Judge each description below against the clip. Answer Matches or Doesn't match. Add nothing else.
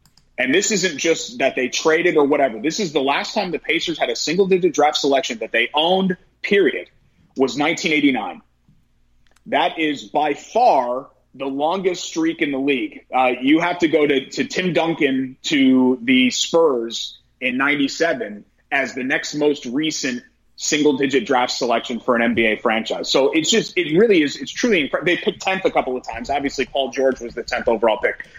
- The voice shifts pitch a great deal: Matches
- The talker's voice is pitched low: Doesn't match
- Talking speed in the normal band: Matches